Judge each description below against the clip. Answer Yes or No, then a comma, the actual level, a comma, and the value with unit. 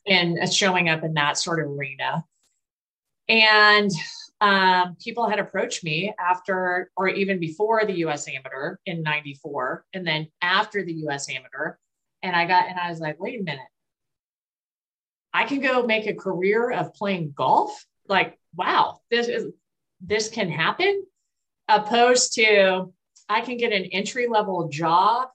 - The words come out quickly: No, average, 150 wpm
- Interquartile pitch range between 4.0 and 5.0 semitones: Yes, average, 4.3 semitones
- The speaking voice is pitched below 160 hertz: No, high, 190 Hz